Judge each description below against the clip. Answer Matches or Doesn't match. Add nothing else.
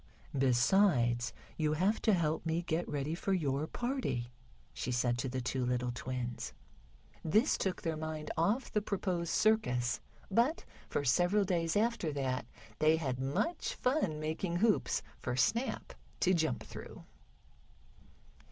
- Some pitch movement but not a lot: Doesn't match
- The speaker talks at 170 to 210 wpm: Doesn't match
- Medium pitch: Matches